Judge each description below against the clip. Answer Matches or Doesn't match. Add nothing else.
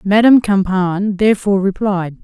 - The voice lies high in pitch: Matches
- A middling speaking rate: Doesn't match